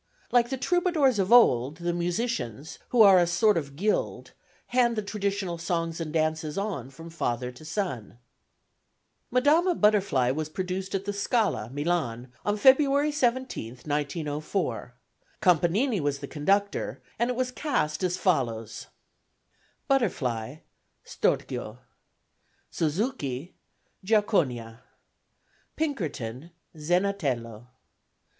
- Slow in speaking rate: Yes, slow, 110 wpm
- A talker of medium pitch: Yes, medium, 175 Hz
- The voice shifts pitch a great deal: Yes, wide, 7.0 semitones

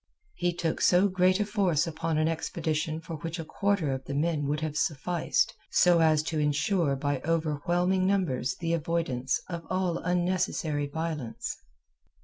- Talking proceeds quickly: No, average, 155 wpm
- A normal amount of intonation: Yes, average, 3.0 semitones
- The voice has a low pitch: No, medium, 165 Hz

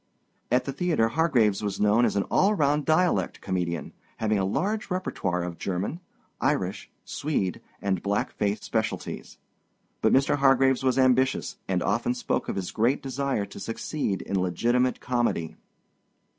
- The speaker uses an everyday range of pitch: No, wide, 5.7 semitones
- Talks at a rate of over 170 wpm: No, average, 150 wpm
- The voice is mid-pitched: No, low, 120 Hz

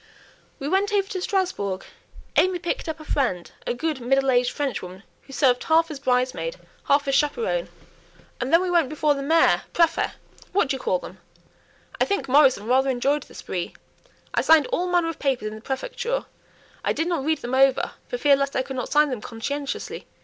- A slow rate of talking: No, average, 200 wpm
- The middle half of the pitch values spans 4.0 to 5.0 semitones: Yes, average, 4.7 semitones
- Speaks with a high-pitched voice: Yes, very high, 285 Hz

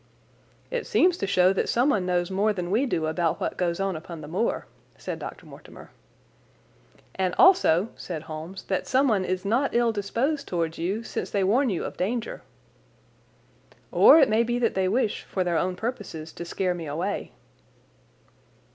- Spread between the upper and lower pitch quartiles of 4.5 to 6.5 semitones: Yes, average, 4.9 semitones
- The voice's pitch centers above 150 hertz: Yes, high, 190 Hz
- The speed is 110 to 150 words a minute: No, average, 175 wpm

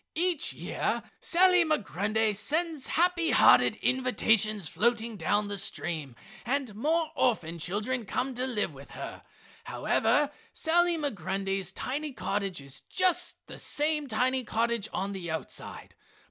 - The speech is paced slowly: Yes, slow, 130 wpm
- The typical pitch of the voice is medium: No, high, 235 Hz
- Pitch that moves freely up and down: Yes, wide, 7.1 semitones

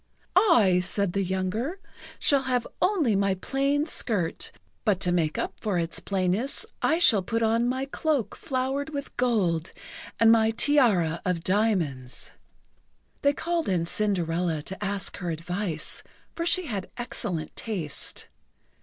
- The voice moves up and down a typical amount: No, wide, 6.5 semitones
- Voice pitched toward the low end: No, high, 205 Hz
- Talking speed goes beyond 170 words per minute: No, average, 140 wpm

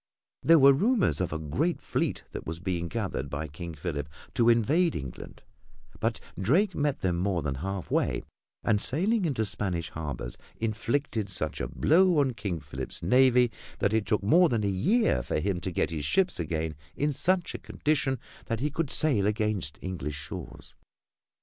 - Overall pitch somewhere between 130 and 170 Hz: No, low, 105 Hz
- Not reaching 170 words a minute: No, average, 175 wpm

